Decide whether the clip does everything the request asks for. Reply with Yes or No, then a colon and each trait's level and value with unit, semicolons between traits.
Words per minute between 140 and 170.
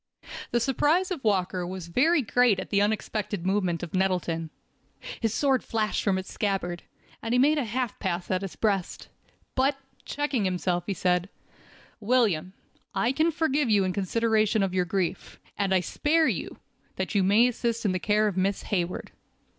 No: average, 180 wpm